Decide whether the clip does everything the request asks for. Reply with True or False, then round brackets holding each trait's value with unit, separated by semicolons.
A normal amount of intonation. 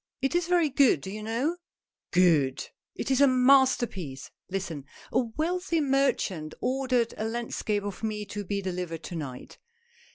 False (6.8 semitones)